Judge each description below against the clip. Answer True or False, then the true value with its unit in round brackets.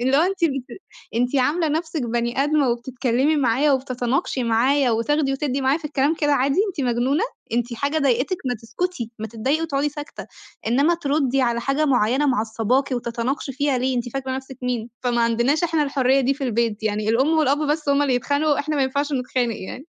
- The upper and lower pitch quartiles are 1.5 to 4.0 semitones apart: True (3.2 semitones)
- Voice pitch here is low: False (265 Hz)